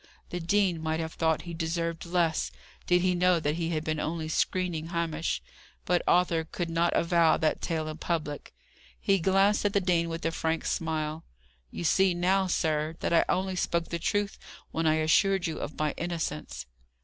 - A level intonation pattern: Yes, narrow, 1.9 semitones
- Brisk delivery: No, average, 185 wpm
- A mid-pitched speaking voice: Yes, medium, 165 Hz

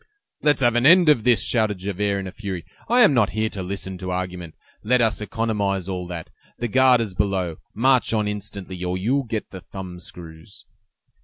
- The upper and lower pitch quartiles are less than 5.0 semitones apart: Yes, average, 4.3 semitones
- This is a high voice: No, low, 100 Hz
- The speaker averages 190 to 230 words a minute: Yes, average, 200 wpm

